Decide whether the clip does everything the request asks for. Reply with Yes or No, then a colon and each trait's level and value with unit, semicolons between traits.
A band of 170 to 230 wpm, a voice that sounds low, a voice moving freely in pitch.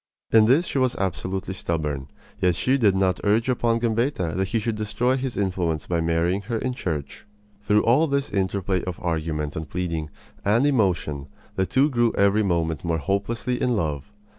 Yes: average, 180 wpm; low, 100 Hz; wide, 5.8 semitones